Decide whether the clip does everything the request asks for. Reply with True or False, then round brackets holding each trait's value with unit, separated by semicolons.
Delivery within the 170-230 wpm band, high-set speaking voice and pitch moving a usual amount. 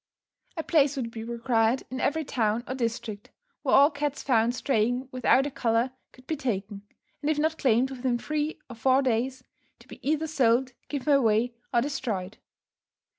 True (175 wpm; 255 Hz; 3.6 semitones)